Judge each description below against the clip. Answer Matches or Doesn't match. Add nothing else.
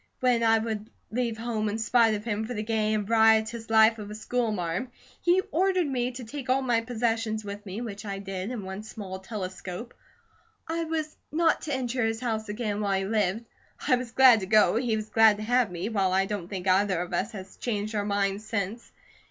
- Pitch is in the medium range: Doesn't match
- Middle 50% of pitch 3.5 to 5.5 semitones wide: Doesn't match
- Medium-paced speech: Doesn't match